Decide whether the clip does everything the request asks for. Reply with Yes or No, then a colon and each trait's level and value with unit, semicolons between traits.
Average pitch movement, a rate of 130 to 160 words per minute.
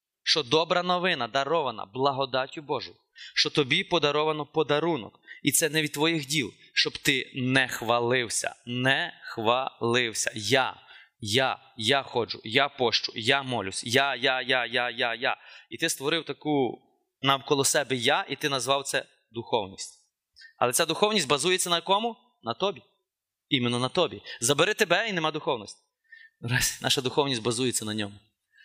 Yes: average, 4.5 semitones; average, 150 wpm